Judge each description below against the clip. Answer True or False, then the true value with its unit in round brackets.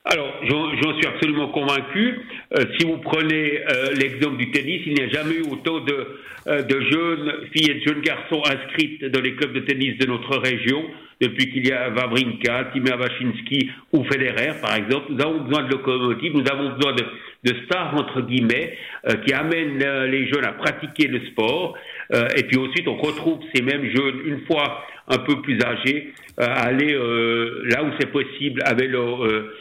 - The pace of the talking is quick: False (195 wpm)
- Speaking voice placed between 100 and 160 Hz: True (140 Hz)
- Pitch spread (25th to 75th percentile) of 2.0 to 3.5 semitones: True (2.7 semitones)